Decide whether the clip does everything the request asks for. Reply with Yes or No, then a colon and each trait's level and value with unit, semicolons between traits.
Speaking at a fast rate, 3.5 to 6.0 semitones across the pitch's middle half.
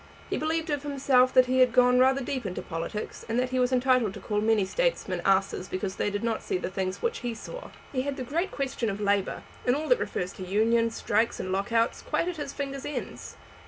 Yes: fast, 235 wpm; average, 5.1 semitones